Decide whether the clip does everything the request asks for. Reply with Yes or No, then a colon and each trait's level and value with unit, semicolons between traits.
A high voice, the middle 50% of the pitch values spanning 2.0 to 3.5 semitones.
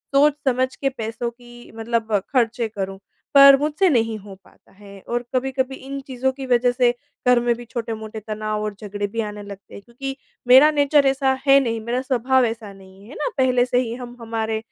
Yes: high, 240 Hz; average, 3.1 semitones